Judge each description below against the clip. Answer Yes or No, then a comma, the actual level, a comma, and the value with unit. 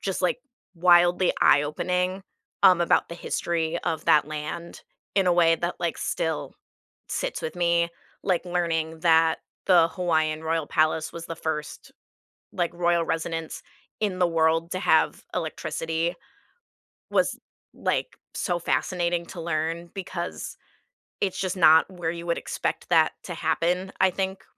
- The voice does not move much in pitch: Yes, narrow, 1.7 semitones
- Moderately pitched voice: Yes, medium, 170 Hz